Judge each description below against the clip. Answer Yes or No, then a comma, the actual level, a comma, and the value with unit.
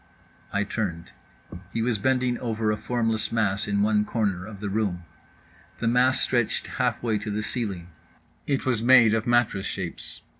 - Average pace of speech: Yes, average, 165 wpm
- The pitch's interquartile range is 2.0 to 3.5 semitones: Yes, average, 2.8 semitones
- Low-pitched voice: Yes, low, 110 Hz